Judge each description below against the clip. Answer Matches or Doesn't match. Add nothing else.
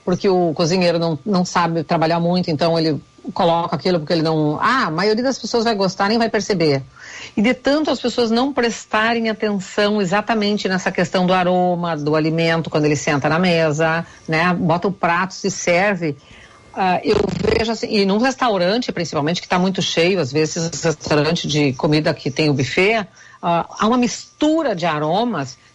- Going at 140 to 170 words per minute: Doesn't match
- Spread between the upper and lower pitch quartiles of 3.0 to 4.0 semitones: Doesn't match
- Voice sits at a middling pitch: Matches